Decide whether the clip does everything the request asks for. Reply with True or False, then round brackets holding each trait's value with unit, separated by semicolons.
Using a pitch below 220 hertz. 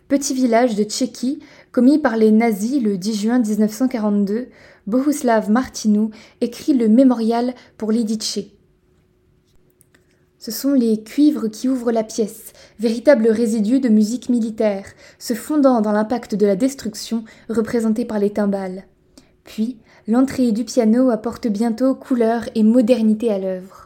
False (230 Hz)